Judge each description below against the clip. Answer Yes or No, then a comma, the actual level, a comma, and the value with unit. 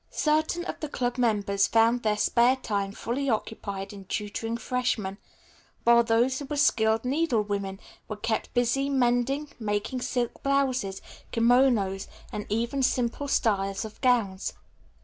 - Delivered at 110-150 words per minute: Yes, slow, 135 wpm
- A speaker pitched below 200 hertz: No, high, 235 Hz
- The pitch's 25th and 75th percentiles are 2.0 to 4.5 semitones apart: Yes, average, 3.8 semitones